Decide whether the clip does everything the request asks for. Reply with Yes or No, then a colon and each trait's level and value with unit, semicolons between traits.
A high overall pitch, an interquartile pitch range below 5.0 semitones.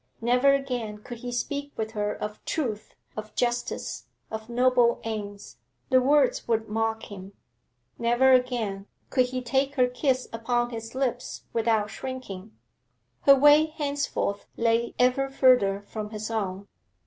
Yes: high, 240 Hz; average, 3.0 semitones